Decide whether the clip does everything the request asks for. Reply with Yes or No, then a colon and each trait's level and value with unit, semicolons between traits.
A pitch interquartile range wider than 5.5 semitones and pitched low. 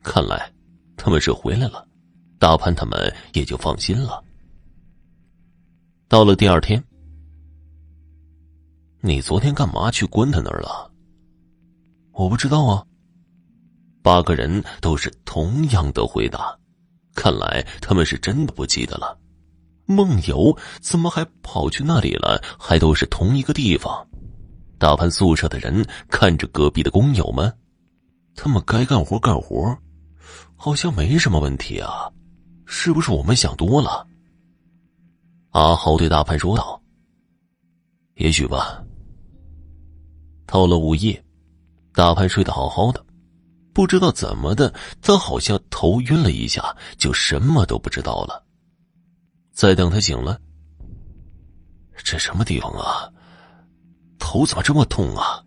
Yes: wide, 8.0 semitones; very low, 85 Hz